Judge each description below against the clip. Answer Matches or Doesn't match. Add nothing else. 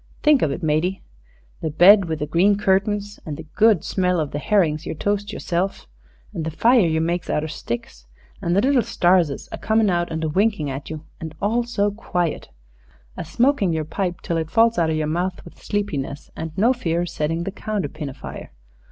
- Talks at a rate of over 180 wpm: Matches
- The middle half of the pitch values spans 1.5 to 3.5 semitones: Doesn't match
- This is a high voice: Doesn't match